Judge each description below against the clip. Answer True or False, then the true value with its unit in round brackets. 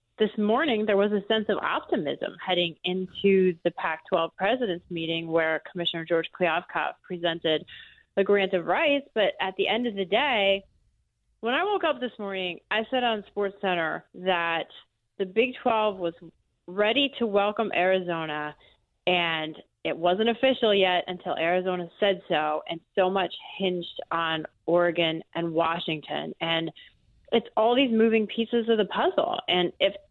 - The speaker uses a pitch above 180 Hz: True (190 Hz)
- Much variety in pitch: False (4.5 semitones)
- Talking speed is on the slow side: False (155 wpm)